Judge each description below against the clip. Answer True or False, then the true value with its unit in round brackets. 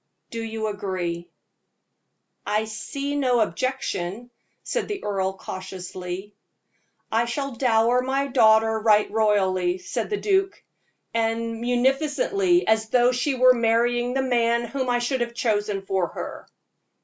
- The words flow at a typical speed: False (130 wpm)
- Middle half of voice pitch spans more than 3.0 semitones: True (3.6 semitones)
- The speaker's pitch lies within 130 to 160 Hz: False (230 Hz)